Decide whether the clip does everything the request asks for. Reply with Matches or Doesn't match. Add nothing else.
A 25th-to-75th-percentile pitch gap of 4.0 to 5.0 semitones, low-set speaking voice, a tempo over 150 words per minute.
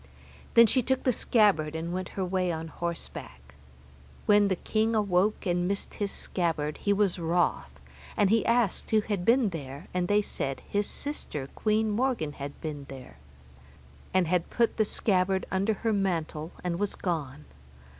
Doesn't match